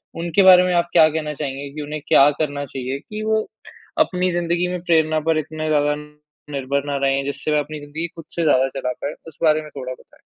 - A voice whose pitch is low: No, medium, 155 Hz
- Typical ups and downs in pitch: Yes, average, 3.1 semitones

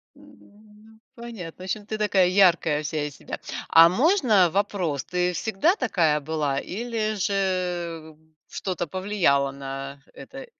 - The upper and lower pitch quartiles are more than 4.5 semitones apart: Yes, average, 5.0 semitones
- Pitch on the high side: No, medium, 180 Hz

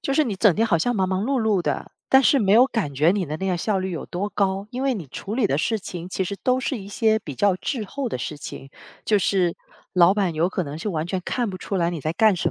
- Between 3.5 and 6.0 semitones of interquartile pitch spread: Yes, average, 4.2 semitones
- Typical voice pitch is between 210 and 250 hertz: No, high, 195 Hz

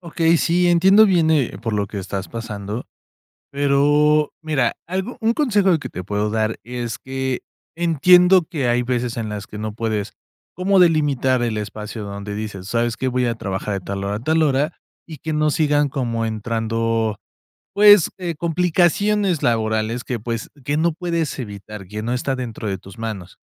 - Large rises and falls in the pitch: Yes, wide, 6.9 semitones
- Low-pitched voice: Yes, low, 125 Hz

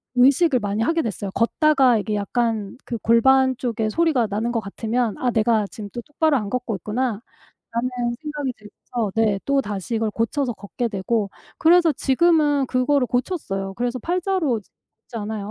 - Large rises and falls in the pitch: No, average, 4.4 semitones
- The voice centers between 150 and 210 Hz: No, high, 240 Hz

